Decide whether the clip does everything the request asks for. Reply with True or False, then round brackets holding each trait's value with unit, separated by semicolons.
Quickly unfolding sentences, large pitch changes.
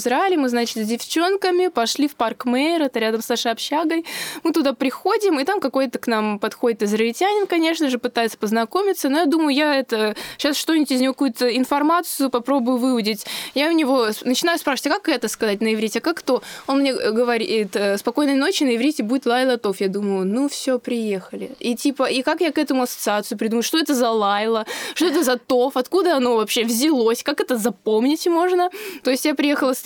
False (200 wpm; 4.8 semitones)